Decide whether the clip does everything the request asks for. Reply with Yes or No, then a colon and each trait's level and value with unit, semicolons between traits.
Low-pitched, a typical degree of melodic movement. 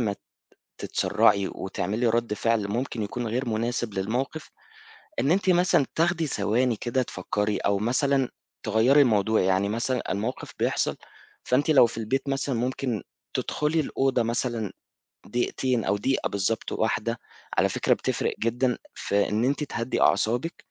Yes: low, 120 Hz; average, 3.7 semitones